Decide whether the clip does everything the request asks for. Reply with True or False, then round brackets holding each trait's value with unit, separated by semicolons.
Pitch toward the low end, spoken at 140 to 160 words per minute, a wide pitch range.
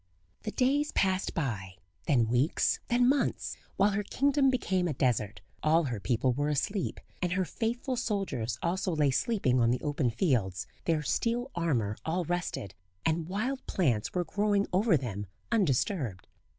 False (165 Hz; 155 wpm; 8.8 semitones)